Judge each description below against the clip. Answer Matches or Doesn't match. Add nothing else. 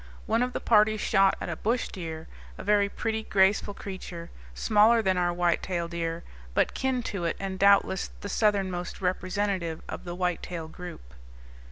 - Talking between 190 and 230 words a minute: Doesn't match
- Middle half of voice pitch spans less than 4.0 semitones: Matches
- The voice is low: Doesn't match